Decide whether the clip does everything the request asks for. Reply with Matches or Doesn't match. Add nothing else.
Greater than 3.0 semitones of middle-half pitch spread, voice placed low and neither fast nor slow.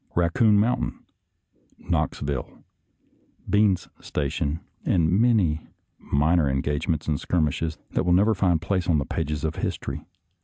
Doesn't match